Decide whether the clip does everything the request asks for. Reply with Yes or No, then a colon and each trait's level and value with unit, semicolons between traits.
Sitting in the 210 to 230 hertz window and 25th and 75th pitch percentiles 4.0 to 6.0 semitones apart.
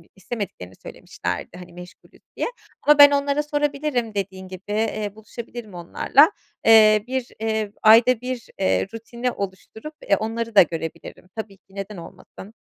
Yes: high, 220 Hz; average, 4.3 semitones